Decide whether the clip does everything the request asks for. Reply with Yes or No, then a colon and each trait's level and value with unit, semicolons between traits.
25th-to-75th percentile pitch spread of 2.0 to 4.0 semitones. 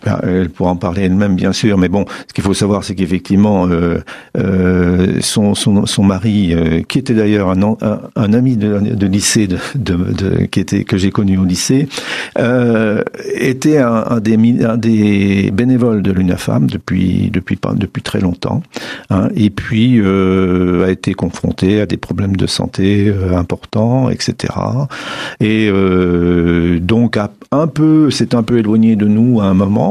Yes: average, 3.4 semitones